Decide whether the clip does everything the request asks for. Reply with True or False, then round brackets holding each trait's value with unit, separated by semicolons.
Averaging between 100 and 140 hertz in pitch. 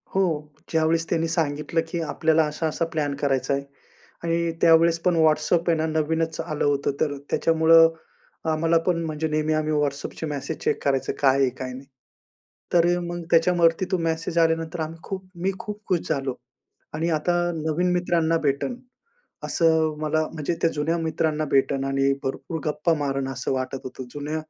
False (160 Hz)